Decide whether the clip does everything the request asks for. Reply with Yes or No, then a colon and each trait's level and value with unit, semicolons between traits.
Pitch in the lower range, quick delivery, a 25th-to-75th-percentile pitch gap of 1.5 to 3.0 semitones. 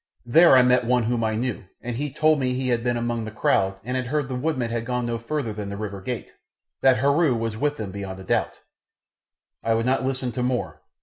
Yes: low, 120 Hz; fast, 240 wpm; narrow, 2.5 semitones